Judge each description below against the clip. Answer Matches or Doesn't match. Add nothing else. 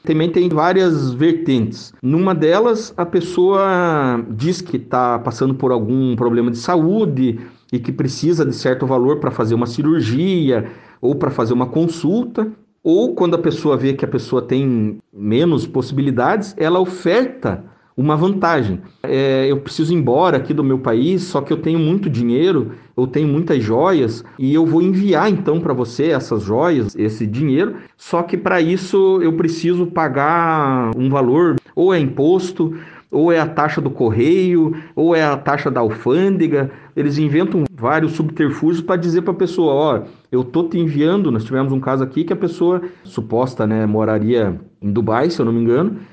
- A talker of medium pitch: Matches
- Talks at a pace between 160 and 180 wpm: Matches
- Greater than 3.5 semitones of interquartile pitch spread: Matches